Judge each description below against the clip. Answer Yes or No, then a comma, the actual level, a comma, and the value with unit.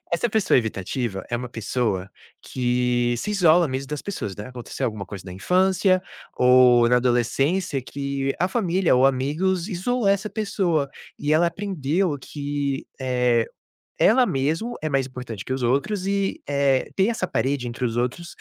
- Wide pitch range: Yes, wide, 6.9 semitones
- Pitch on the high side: No, medium, 140 Hz